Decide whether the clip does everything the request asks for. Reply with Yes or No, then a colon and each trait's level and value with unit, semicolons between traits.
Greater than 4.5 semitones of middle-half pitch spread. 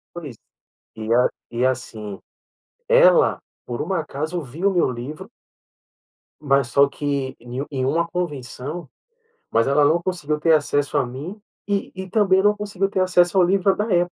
Yes: wide, 5.5 semitones